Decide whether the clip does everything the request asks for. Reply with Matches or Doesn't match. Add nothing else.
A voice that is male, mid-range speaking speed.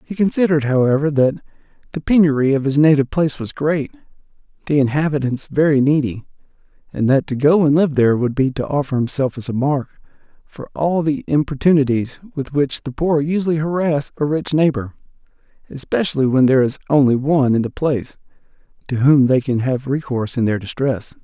Matches